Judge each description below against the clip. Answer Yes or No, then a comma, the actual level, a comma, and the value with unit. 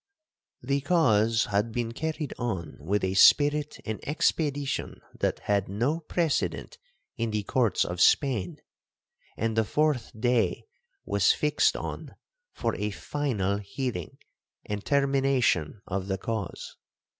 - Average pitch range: No, wide, 5.7 semitones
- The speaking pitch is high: No, low, 115 Hz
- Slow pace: Yes, slow, 125 wpm